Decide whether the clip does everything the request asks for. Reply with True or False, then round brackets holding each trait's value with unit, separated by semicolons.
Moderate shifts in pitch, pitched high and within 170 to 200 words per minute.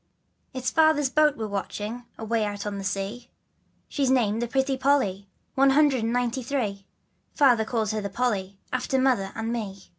True (4.4 semitones; 235 Hz; 175 wpm)